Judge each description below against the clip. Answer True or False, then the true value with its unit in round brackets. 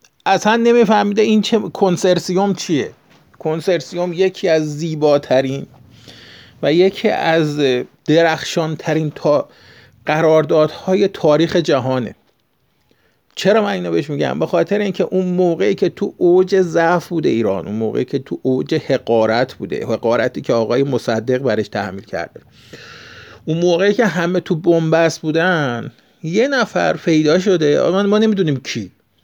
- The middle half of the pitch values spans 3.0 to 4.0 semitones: False (4.5 semitones)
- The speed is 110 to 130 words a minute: True (125 wpm)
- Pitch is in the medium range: True (165 Hz)